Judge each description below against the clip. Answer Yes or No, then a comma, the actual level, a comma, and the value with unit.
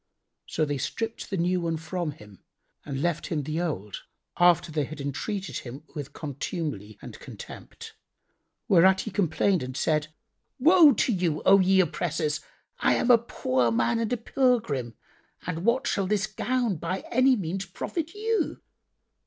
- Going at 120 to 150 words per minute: No, average, 160 wpm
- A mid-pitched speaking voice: Yes, medium, 175 Hz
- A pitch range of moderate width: No, wide, 6.6 semitones